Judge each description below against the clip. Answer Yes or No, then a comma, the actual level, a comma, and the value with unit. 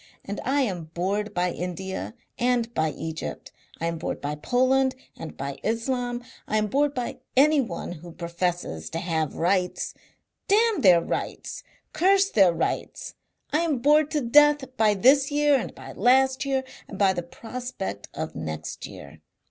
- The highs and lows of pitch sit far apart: Yes, wide, 7.7 semitones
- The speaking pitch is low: No, high, 220 Hz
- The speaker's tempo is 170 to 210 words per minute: No, average, 160 wpm